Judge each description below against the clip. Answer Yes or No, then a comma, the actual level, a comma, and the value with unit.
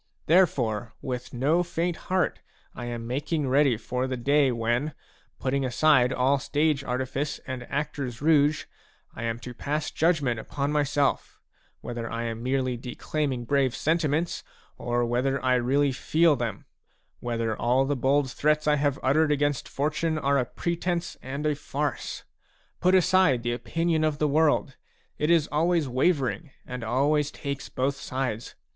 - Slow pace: No, average, 155 wpm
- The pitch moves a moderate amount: Yes, average, 3.4 semitones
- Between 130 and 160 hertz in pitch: Yes, medium, 140 Hz